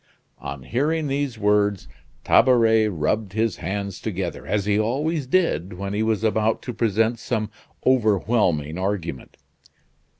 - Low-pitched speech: Yes, low, 110 Hz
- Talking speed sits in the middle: No, slow, 130 wpm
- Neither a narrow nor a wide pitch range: Yes, average, 3.3 semitones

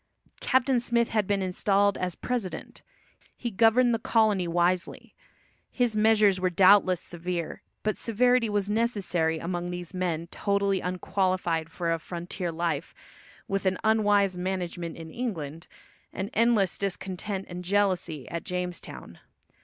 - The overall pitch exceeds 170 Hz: Yes, high, 190 Hz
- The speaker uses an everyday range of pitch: Yes, average, 3.2 semitones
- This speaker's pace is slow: Yes, slow, 130 wpm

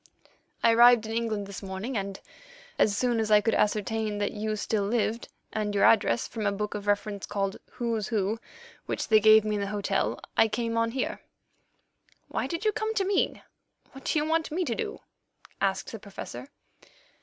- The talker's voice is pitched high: Yes, high, 215 Hz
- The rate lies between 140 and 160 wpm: No, average, 190 wpm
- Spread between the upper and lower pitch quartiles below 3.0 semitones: Yes, narrow, 2.6 semitones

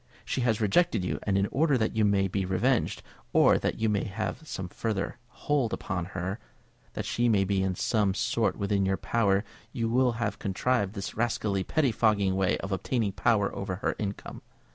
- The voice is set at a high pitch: No, low, 105 Hz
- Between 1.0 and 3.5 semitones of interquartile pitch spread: Yes, average, 3.2 semitones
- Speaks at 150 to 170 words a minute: No, average, 185 wpm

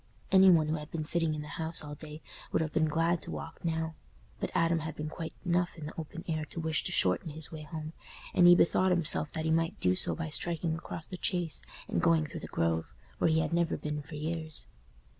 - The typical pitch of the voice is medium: Yes, medium, 160 Hz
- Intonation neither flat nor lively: No, narrow, 1.6 semitones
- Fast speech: Yes, fast, 240 wpm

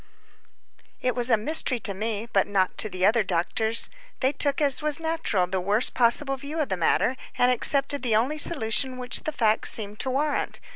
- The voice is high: Yes, high, 245 Hz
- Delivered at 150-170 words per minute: No, average, 195 wpm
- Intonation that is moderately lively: Yes, average, 5.0 semitones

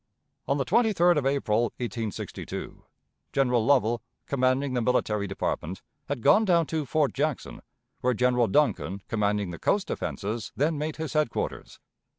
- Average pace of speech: Yes, average, 145 wpm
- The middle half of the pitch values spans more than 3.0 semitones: Yes, average, 5.2 semitones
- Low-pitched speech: Yes, low, 130 Hz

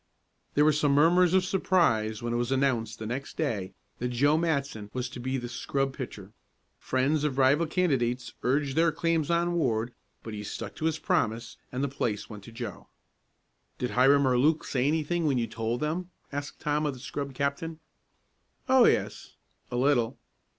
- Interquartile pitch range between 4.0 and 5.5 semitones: Yes, average, 4.3 semitones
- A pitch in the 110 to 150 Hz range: Yes, low, 135 Hz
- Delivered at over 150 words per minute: Yes, average, 185 wpm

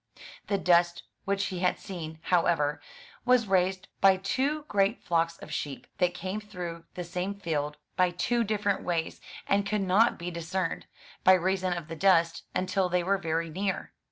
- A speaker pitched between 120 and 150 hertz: No, medium, 180 Hz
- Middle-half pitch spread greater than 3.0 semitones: No, average, 2.7 semitones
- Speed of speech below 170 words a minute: No, average, 195 wpm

